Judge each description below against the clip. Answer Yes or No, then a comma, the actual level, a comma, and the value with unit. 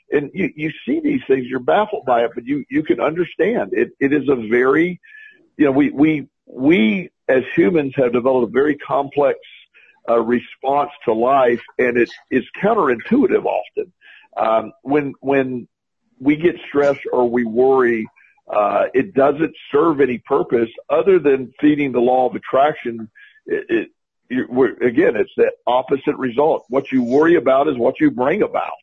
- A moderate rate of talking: Yes, average, 170 wpm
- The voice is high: No, medium, 160 Hz